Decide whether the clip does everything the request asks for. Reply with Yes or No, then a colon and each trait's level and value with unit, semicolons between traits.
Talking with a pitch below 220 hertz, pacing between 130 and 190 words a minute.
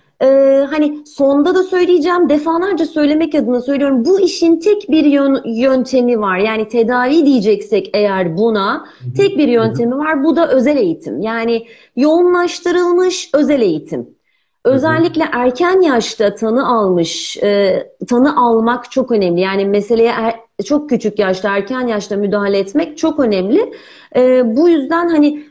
No: very high, 265 Hz; average, 135 wpm